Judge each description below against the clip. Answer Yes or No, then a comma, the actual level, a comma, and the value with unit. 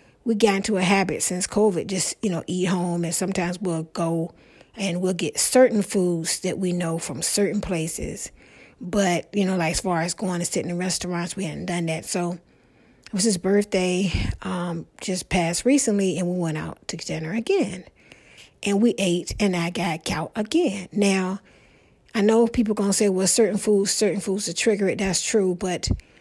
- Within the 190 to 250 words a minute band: Yes, average, 195 wpm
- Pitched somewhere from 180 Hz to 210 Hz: Yes, medium, 185 Hz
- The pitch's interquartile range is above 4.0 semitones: No, average, 2.9 semitones